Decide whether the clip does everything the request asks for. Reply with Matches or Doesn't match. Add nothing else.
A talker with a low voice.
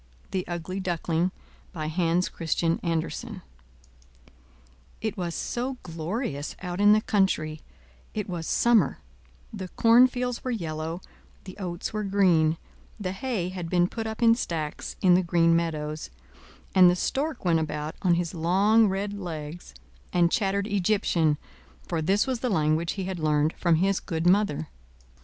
Doesn't match